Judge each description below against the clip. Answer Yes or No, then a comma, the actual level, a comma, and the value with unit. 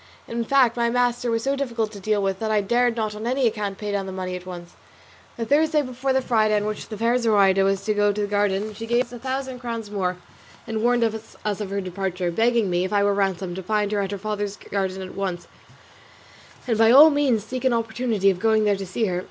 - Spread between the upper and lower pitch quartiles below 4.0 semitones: Yes, average, 3.3 semitones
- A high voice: Yes, high, 215 Hz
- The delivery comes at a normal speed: No, fast, 250 wpm